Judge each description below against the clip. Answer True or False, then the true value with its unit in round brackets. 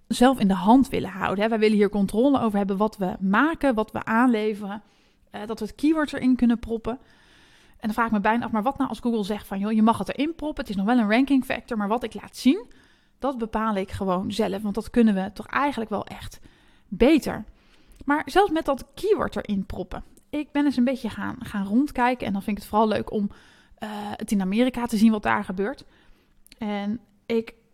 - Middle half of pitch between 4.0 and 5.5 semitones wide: False (3.6 semitones)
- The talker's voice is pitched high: True (225 Hz)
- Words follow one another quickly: True (225 wpm)